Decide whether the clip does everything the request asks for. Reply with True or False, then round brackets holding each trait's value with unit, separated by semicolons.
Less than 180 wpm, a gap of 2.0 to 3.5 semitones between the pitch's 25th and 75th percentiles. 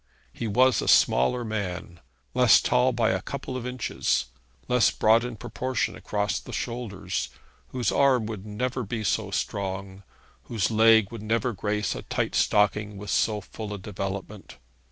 True (155 wpm; 3.0 semitones)